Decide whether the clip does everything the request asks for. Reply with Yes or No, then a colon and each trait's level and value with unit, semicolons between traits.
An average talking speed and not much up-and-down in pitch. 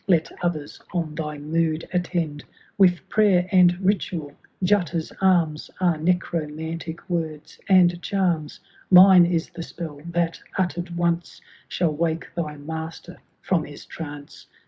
No: slow, 125 wpm; narrow, 2.2 semitones